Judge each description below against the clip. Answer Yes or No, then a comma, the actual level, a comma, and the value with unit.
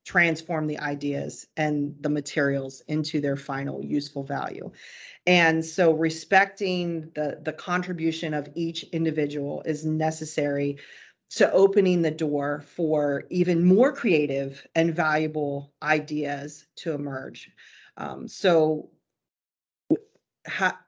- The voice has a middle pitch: Yes, medium, 155 Hz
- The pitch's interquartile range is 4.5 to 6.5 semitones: No, narrow, 2.5 semitones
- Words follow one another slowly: Yes, slow, 110 wpm